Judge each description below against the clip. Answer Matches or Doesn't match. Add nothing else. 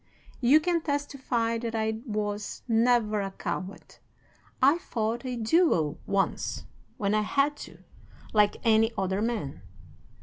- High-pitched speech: Matches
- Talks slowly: Matches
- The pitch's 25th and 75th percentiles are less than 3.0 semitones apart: Doesn't match